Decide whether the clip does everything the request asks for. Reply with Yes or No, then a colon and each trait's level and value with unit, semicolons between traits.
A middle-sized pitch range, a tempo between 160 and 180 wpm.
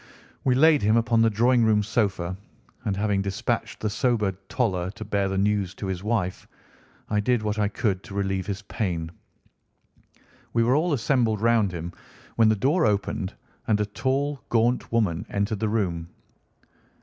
Yes: average, 3.1 semitones; average, 170 wpm